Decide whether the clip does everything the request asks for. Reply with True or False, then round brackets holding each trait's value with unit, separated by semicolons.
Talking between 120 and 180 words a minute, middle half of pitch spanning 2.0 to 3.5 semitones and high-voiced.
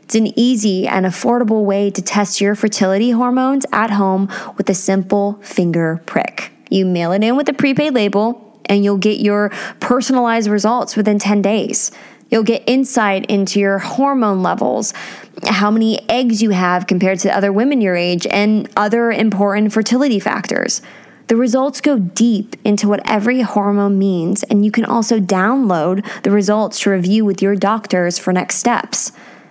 True (165 wpm; 2.8 semitones; 210 Hz)